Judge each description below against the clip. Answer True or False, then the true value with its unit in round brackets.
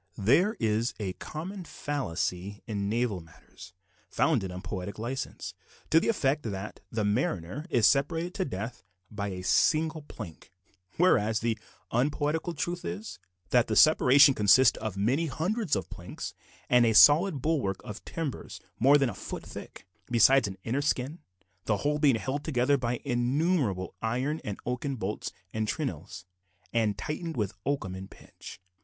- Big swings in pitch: True (6.3 semitones)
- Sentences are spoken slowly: False (155 wpm)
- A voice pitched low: True (125 Hz)